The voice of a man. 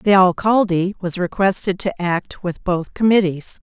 No: female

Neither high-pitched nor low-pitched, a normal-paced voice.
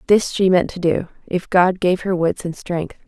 No: medium, 180 Hz; fast, 235 wpm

